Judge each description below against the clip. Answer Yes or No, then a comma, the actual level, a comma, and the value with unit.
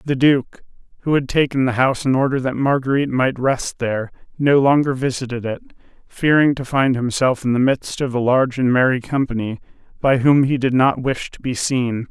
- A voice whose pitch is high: No, low, 130 Hz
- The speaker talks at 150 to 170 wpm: No, average, 200 wpm